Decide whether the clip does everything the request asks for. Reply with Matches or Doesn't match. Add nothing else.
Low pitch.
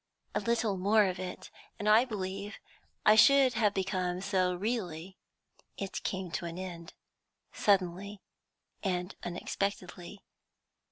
Doesn't match